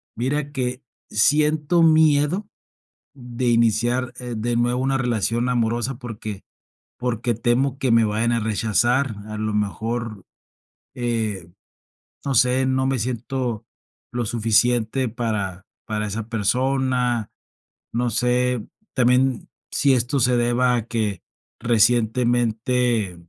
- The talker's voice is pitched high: No, low, 120 Hz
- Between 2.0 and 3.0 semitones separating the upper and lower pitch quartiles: Yes, narrow, 2.4 semitones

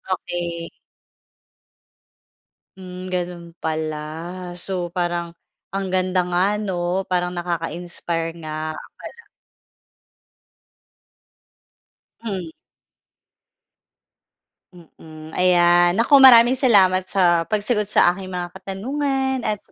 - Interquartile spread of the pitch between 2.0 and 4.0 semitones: Yes, narrow, 2.4 semitones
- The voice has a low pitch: No, medium, 180 Hz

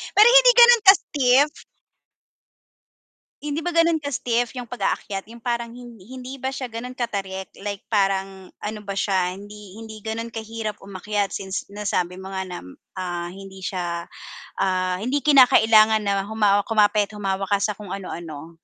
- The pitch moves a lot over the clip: No, average, 4.1 semitones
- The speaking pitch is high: Yes, high, 210 Hz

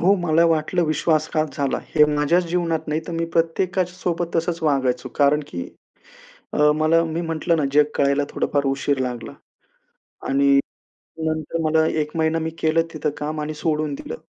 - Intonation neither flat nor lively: No, narrow, 2.0 semitones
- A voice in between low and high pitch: Yes, medium, 155 Hz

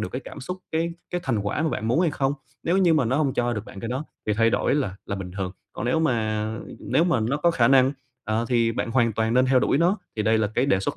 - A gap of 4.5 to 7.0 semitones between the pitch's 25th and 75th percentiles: Yes, average, 4.8 semitones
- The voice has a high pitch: No, low, 125 Hz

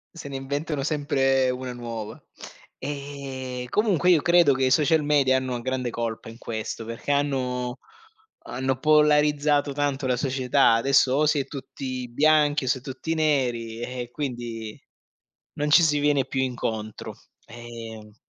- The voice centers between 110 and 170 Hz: Yes, low, 135 Hz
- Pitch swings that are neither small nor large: Yes, average, 3.0 semitones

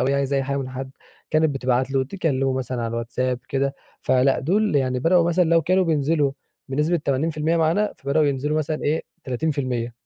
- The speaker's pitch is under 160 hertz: Yes, medium, 140 Hz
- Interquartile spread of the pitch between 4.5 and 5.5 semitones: No, average, 3.4 semitones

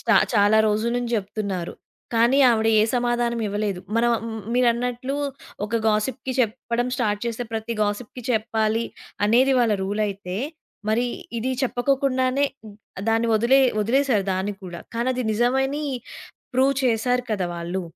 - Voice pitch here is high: Yes, high, 235 Hz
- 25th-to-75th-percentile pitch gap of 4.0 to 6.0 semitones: No, average, 2.8 semitones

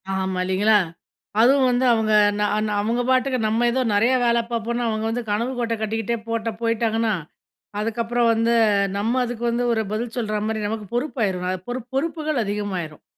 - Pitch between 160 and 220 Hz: No, high, 230 Hz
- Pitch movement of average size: No, narrow, 2.1 semitones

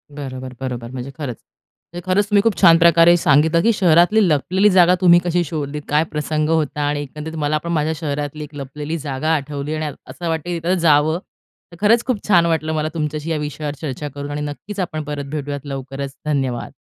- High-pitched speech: No, medium, 155 Hz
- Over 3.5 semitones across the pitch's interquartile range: No, average, 2.8 semitones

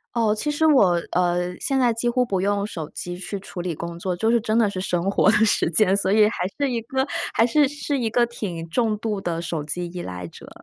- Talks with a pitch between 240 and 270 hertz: No, high, 205 Hz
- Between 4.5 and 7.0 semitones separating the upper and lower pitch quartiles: Yes, average, 5.0 semitones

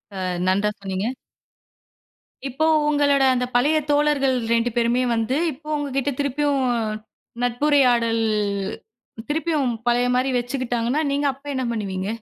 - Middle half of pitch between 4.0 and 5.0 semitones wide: No, average, 3.5 semitones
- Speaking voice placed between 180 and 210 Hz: No, very high, 255 Hz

